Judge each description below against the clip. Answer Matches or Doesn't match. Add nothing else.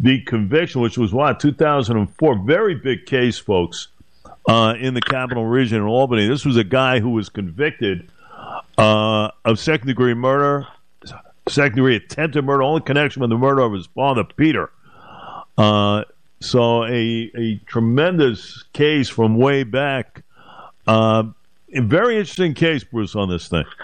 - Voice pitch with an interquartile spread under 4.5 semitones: Matches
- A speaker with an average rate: Matches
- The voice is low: Matches